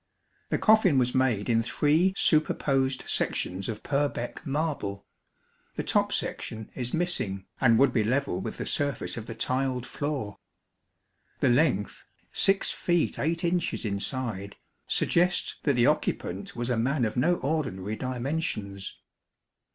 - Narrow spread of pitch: No, average, 5.3 semitones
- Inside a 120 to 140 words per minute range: Yes, slow, 135 wpm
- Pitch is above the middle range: No, low, 130 Hz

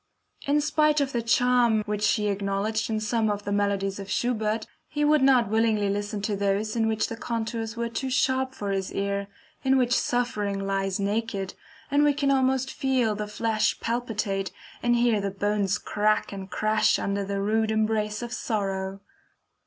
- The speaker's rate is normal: Yes, average, 175 wpm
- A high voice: Yes, high, 215 Hz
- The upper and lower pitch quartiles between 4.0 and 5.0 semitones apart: No, average, 3.1 semitones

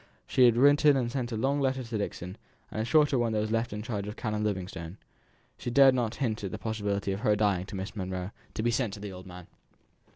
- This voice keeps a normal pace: No, fast, 240 wpm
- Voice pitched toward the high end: No, low, 110 Hz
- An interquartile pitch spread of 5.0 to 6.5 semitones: No, average, 3.6 semitones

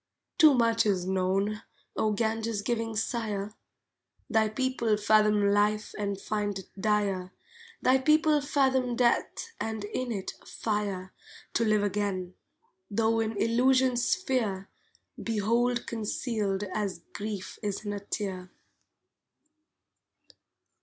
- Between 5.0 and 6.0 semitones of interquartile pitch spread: No, narrow, 2.6 semitones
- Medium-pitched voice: No, high, 215 Hz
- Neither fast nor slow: No, slow, 110 wpm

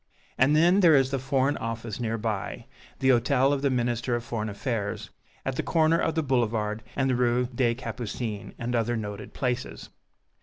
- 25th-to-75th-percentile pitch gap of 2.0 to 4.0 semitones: Yes, average, 2.7 semitones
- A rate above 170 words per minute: Yes, average, 185 wpm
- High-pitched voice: No, low, 125 Hz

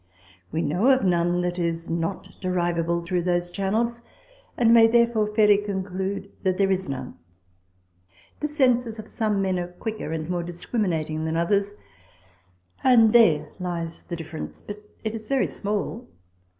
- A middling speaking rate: Yes, average, 150 wpm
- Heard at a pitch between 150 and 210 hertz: Yes, high, 190 Hz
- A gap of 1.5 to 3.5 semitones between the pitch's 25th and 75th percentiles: No, average, 4.3 semitones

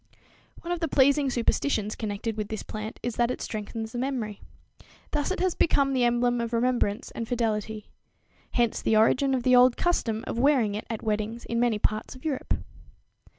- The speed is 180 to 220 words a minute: Yes, average, 190 wpm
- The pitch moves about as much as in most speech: Yes, average, 3.2 semitones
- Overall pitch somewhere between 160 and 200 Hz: No, high, 235 Hz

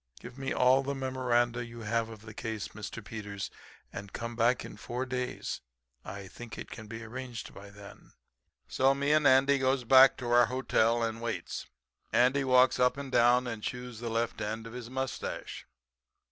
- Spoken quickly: No, average, 185 wpm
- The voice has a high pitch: No, low, 120 Hz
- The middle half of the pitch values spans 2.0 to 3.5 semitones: Yes, narrow, 2.5 semitones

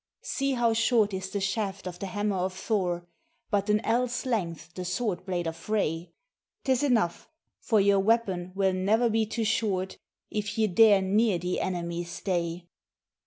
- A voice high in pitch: Yes, high, 195 Hz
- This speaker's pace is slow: No, average, 165 wpm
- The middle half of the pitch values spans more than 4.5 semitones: No, average, 3.6 semitones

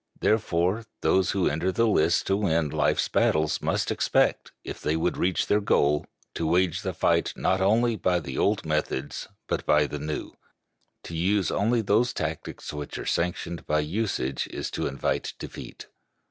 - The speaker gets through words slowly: No, average, 170 wpm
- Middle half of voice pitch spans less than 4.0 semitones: No, average, 4.8 semitones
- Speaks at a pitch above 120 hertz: No, very low, 85 Hz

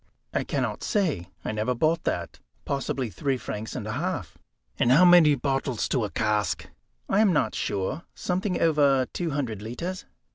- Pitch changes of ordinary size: No, wide, 7.0 semitones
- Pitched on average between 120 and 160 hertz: Yes, low, 135 Hz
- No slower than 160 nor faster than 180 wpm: Yes, average, 170 wpm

